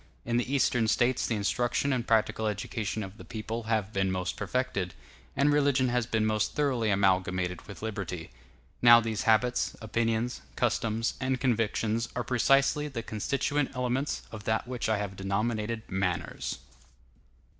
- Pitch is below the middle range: Yes, low, 115 Hz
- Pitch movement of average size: Yes, average, 3.0 semitones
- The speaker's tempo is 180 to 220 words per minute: No, average, 150 wpm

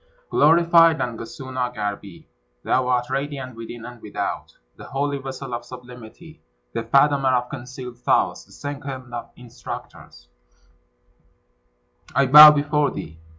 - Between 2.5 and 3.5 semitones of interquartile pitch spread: Yes, average, 2.9 semitones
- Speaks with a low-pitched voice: Yes, low, 130 Hz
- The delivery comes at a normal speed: No, slow, 120 wpm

